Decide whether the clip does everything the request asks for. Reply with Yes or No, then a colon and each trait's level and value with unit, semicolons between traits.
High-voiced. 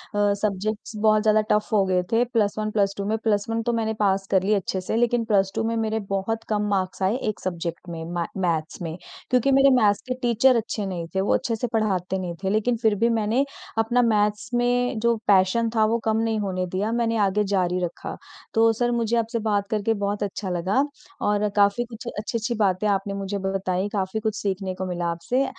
Yes: high, 210 Hz